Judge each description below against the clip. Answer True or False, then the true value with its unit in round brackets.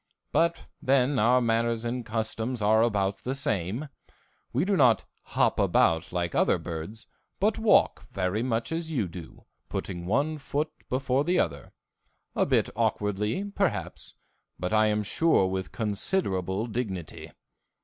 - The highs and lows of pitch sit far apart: True (6.0 semitones)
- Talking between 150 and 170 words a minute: False (140 wpm)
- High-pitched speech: False (115 Hz)